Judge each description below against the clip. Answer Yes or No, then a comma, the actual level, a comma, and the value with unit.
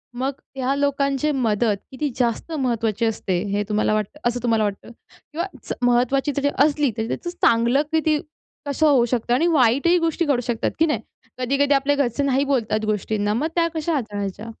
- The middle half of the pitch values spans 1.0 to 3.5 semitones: No, average, 4.1 semitones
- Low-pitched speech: No, very high, 260 Hz